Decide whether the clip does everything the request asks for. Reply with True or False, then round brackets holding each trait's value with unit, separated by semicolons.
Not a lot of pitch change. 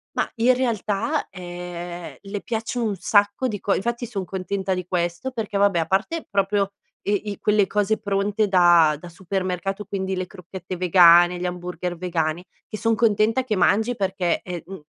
False (3.0 semitones)